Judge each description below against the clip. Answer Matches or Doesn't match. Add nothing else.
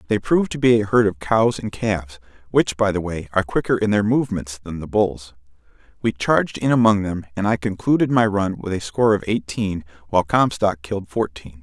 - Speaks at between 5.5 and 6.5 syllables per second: Matches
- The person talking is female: Doesn't match